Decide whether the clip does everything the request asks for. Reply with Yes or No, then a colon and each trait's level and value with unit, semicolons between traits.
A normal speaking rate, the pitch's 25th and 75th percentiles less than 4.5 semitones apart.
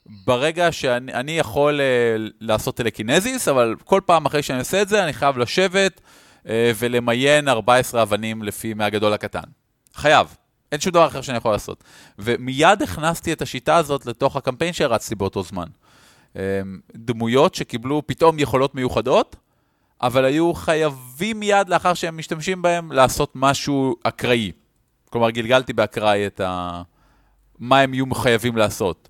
No: average, 135 wpm; wide, 5.5 semitones